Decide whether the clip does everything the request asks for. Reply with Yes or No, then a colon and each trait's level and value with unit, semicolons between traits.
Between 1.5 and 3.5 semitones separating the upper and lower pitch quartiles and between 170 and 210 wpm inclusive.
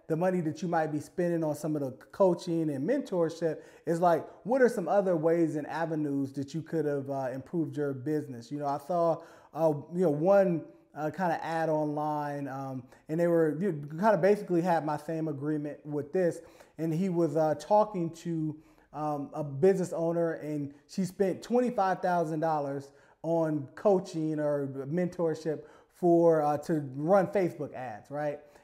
Yes: average, 2.8 semitones; average, 180 wpm